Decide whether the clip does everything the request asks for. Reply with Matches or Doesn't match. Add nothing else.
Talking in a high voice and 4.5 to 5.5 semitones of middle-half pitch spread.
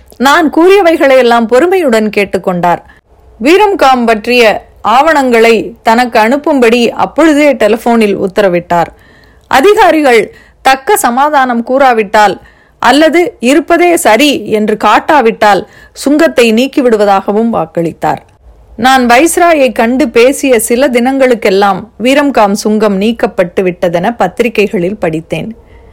Matches